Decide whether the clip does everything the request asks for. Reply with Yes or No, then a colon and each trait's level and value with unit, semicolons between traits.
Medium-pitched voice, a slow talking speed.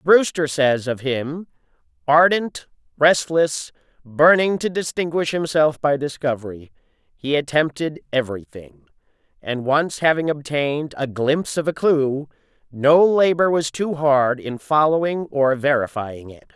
Yes: medium, 145 Hz; slow, 120 wpm